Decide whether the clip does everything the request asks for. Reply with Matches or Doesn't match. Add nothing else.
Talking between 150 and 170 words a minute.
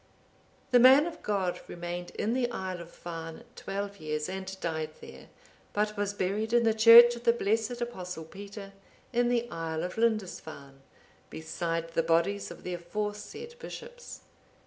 Matches